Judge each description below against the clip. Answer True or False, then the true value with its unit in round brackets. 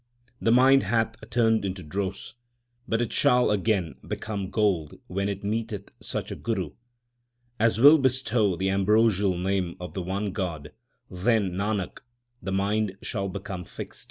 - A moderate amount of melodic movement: True (3.0 semitones)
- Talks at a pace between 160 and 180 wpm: False (150 wpm)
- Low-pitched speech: True (100 Hz)